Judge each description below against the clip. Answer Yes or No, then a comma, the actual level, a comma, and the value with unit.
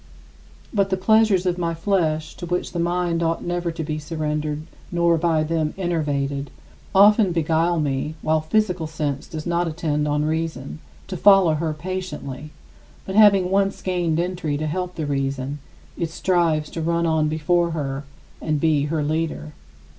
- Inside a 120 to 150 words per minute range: No, average, 160 wpm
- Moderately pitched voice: Yes, medium, 165 Hz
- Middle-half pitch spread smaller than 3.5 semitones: Yes, narrow, 2.6 semitones